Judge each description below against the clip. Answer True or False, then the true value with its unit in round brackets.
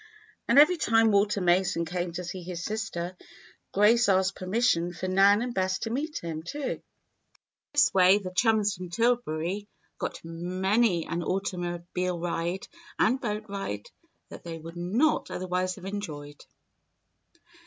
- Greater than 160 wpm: False (145 wpm)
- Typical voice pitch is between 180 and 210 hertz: True (185 Hz)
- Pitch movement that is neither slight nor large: True (3.6 semitones)